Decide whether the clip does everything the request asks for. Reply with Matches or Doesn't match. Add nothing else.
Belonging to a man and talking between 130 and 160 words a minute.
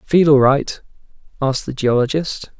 Matches